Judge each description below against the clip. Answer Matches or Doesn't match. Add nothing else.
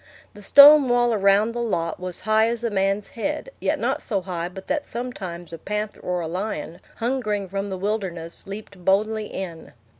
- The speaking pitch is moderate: Doesn't match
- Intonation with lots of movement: Doesn't match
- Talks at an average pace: Matches